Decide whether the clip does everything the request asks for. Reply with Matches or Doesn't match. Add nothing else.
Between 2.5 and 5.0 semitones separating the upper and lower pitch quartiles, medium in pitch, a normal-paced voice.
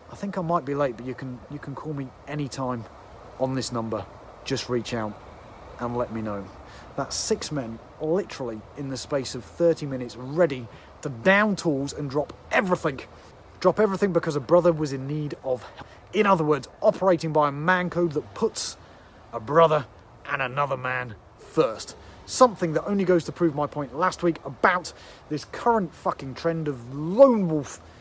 Doesn't match